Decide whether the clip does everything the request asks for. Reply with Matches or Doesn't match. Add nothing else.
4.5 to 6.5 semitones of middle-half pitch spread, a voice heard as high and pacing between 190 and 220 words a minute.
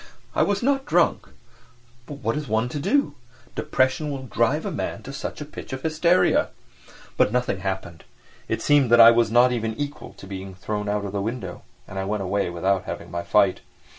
Doesn't match